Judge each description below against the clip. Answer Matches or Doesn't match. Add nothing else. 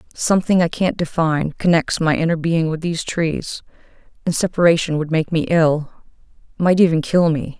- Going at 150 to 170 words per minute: Matches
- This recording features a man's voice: Doesn't match